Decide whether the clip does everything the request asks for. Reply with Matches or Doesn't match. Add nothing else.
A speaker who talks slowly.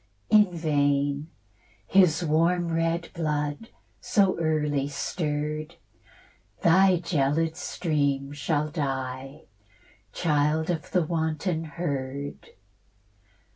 Matches